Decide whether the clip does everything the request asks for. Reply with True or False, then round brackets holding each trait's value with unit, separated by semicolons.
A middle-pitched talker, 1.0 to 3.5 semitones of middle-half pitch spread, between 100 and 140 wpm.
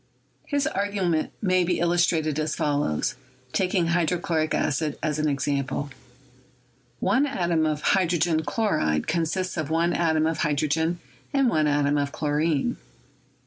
True (160 Hz; 2.8 semitones; 135 wpm)